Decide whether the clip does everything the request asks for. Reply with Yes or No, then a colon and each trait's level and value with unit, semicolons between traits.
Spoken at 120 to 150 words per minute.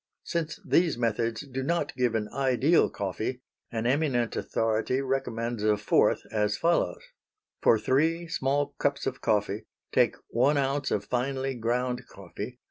Yes: average, 140 wpm